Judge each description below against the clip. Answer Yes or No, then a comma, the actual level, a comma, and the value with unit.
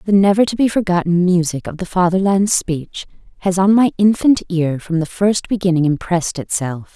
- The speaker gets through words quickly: No, average, 180 wpm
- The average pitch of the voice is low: No, medium, 185 Hz